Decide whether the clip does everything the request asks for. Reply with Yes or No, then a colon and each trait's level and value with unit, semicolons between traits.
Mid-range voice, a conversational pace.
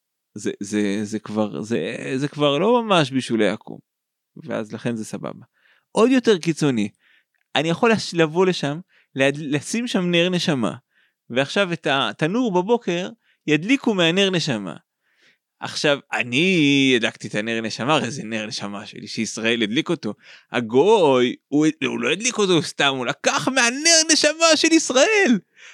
Yes: medium, 155 Hz; average, 140 wpm